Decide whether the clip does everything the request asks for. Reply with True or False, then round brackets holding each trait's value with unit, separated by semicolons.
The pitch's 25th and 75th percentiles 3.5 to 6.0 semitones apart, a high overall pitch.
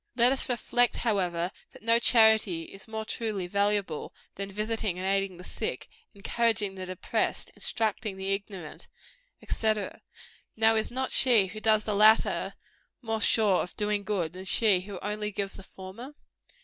False (2.5 semitones; 210 Hz)